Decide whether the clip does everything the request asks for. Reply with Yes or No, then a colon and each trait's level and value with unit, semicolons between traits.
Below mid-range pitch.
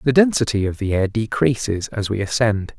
Yes: low, 110 Hz